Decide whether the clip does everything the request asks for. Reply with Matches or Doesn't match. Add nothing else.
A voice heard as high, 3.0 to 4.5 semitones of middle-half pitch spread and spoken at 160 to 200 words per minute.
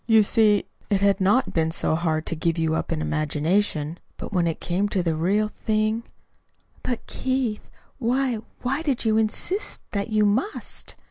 Doesn't match